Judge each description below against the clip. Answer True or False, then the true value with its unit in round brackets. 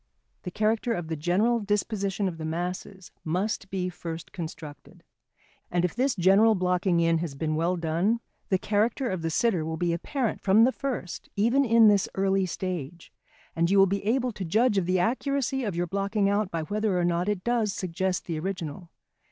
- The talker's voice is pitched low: False (190 Hz)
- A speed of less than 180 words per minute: False (195 wpm)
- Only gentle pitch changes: False (3.9 semitones)